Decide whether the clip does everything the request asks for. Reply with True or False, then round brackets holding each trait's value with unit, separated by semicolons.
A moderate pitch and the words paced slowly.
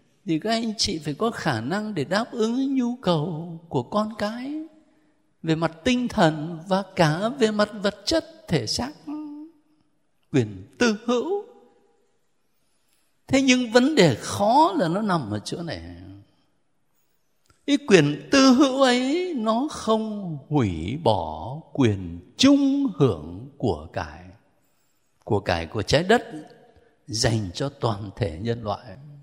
True (175 Hz; 140 wpm)